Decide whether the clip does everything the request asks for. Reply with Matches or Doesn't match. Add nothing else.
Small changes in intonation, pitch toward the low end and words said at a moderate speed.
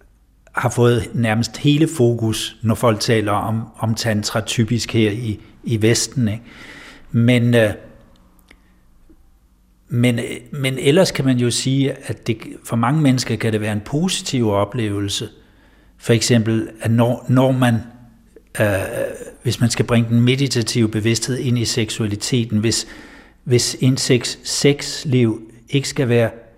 Doesn't match